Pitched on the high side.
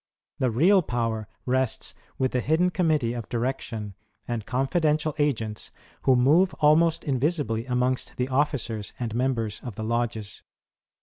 No: low, 125 Hz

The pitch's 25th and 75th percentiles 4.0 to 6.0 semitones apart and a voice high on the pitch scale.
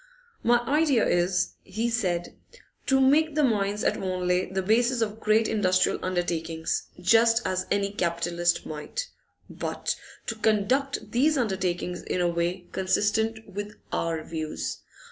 Yes: average, 4.6 semitones; high, 200 Hz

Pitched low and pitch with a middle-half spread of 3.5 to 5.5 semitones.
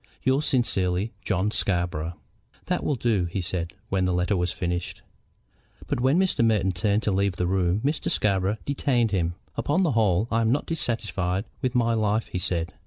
Yes: low, 100 Hz; average, 4.6 semitones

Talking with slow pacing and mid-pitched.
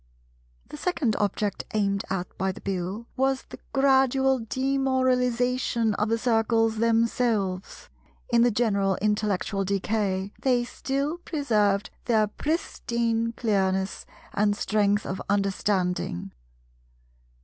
No: slow, 105 wpm; high, 225 Hz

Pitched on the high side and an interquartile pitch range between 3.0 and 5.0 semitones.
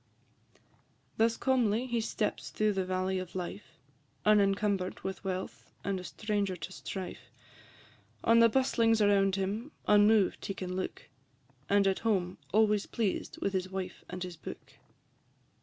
No: high, 200 Hz; narrow, 2.5 semitones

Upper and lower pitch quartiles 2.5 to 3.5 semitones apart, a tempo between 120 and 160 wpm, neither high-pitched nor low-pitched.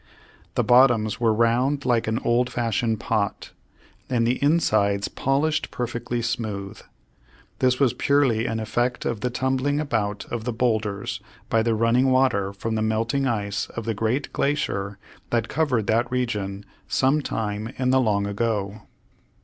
No: average, 2.8 semitones; average, 150 wpm; low, 115 Hz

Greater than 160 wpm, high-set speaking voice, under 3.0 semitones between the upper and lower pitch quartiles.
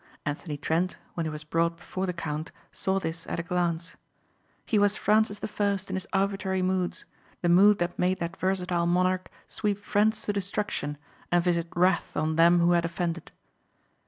No: average, 180 wpm; medium, 180 Hz; narrow, 2.4 semitones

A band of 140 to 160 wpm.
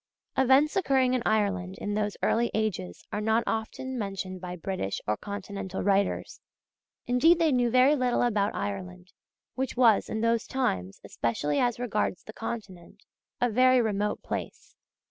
Yes: average, 150 wpm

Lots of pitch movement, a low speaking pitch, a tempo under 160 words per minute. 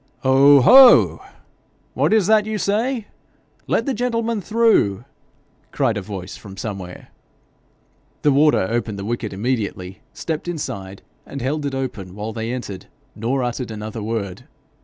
Yes: wide, 8.5 semitones; low, 125 Hz; average, 140 wpm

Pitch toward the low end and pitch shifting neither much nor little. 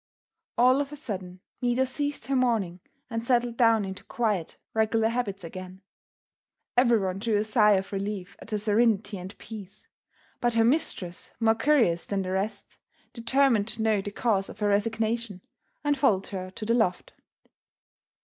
No: high, 220 Hz; average, 3.5 semitones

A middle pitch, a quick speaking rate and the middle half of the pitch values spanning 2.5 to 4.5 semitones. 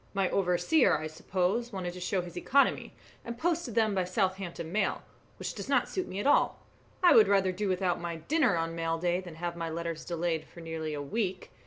Yes: medium, 180 Hz; fast, 215 wpm; average, 3.4 semitones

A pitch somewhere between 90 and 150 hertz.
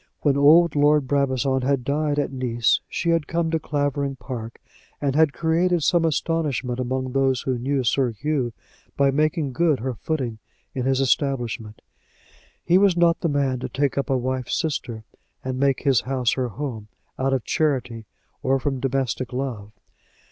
Yes: low, 135 Hz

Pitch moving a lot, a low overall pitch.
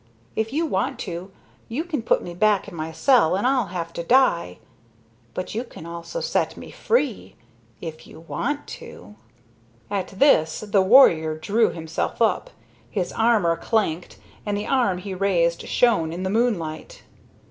No: wide, 5.9 semitones; high, 195 Hz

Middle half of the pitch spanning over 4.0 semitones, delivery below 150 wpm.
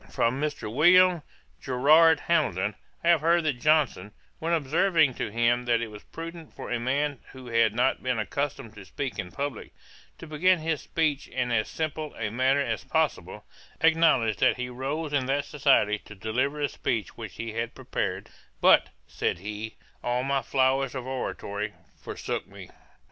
No: average, 4.8 semitones; average, 170 wpm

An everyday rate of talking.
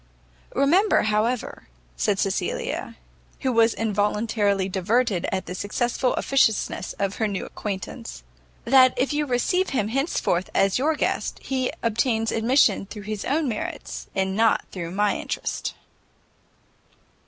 No: slow, 130 wpm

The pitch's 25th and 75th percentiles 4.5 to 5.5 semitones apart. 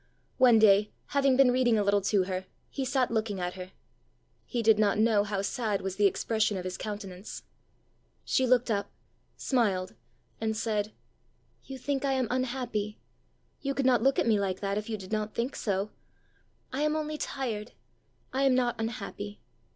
No: average, 4.0 semitones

